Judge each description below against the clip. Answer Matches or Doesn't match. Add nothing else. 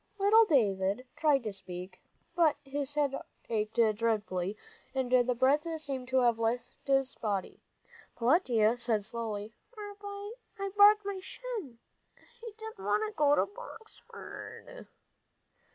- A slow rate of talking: Matches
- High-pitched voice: Matches